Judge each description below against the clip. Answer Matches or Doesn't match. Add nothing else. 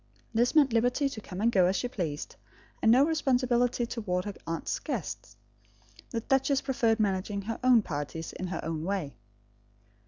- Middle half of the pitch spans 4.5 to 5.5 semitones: Matches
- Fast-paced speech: Doesn't match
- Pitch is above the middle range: Matches